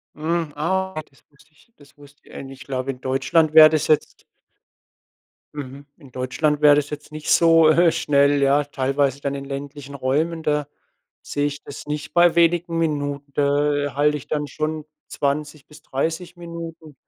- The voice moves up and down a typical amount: No, narrow, 2.0 semitones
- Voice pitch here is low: No, medium, 145 Hz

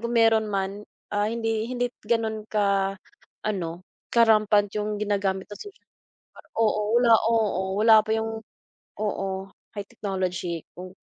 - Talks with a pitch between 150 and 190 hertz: No, high, 210 Hz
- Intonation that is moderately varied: No, narrow, 2.2 semitones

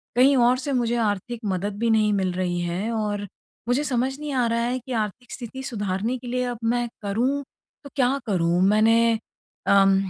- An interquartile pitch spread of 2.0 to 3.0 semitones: No, average, 3.8 semitones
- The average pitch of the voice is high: Yes, high, 230 Hz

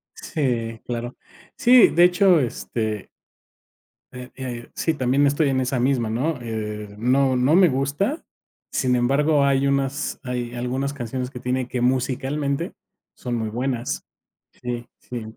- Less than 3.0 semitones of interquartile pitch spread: Yes, narrow, 2.5 semitones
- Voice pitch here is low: Yes, low, 130 Hz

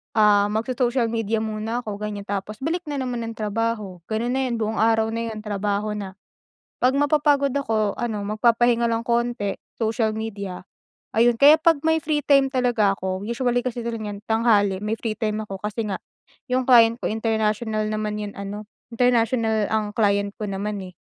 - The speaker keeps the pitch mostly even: Yes, narrow, 2.3 semitones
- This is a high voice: Yes, high, 220 Hz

